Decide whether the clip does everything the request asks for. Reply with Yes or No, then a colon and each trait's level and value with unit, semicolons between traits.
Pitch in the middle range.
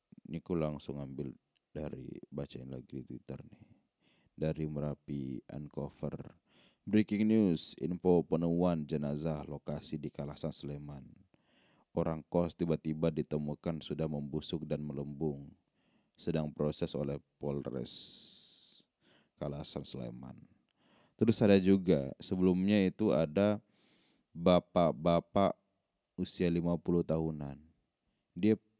No: very low, 80 Hz